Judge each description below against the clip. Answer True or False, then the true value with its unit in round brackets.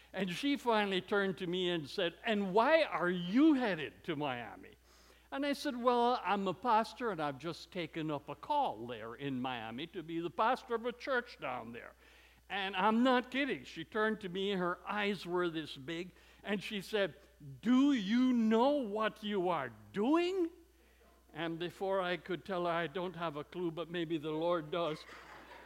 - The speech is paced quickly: False (185 wpm)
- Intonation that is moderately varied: False (5.7 semitones)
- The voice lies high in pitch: True (195 Hz)